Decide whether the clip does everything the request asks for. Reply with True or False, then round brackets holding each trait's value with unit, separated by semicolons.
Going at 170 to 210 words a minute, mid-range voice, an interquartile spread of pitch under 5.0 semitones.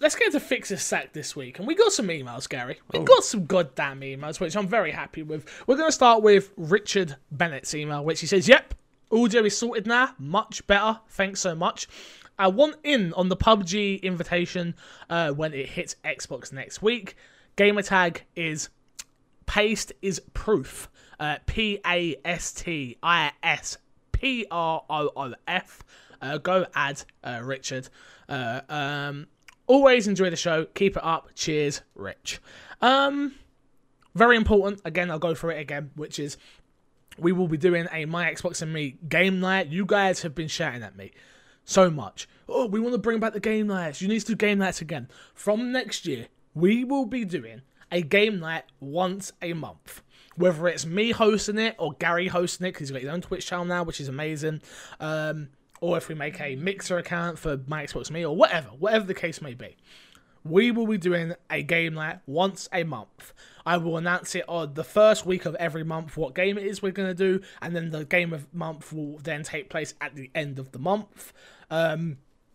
True (190 wpm; 175 Hz; 4.6 semitones)